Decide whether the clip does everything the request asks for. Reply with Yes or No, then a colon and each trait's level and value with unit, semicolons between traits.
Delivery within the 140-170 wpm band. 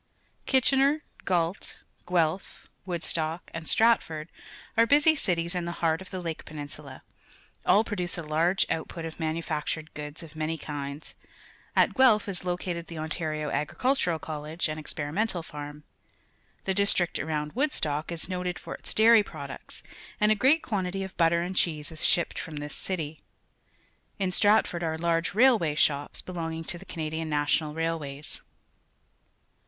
Yes: average, 155 wpm